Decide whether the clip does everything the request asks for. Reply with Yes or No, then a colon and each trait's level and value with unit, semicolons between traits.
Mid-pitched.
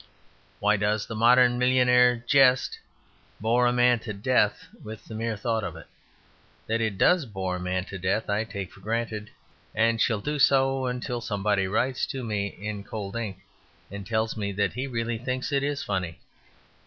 No: low, 110 Hz